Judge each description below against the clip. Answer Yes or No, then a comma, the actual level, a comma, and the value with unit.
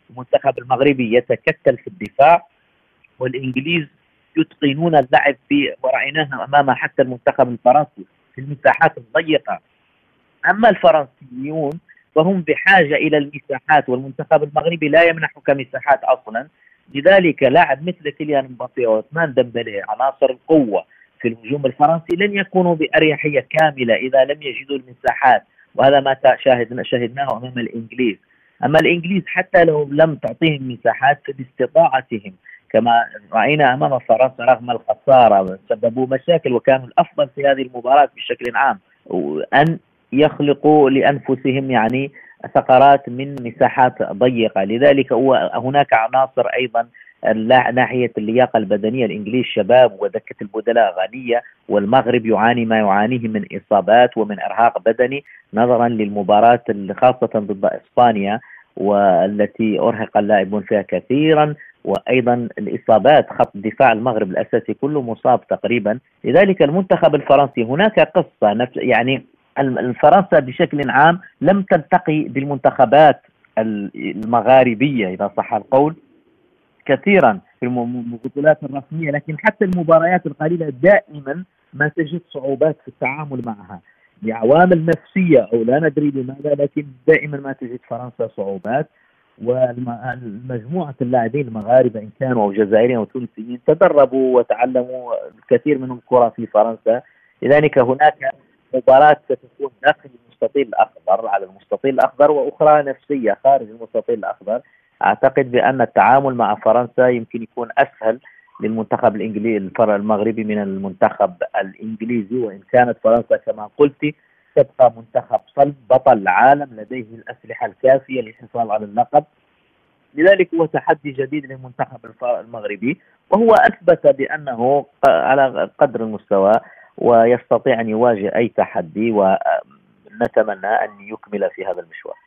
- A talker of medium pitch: No, low, 130 Hz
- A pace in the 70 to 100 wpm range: No, average, 115 wpm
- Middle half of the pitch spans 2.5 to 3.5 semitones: No, average, 4.2 semitones